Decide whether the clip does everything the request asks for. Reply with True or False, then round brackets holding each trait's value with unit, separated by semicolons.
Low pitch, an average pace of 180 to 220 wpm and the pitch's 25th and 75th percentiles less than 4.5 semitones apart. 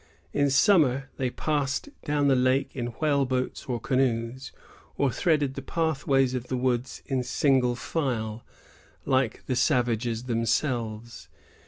False (130 Hz; 135 wpm; 2.5 semitones)